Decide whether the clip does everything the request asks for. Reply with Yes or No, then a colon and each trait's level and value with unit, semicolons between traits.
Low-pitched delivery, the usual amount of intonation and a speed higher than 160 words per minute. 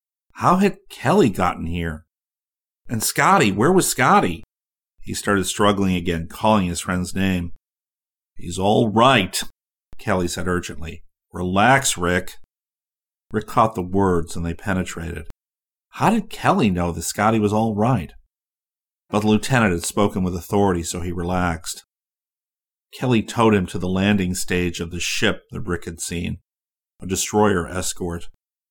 No: very low, 90 Hz; average, 3.1 semitones; average, 145 wpm